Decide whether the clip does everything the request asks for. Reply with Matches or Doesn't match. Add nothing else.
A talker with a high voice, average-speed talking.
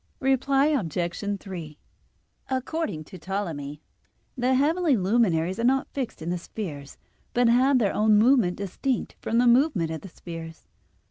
Matches